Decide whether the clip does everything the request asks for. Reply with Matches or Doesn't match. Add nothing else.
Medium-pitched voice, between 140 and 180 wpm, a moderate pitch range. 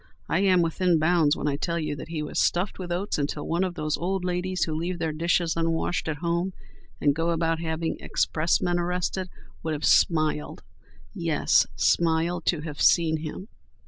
Doesn't match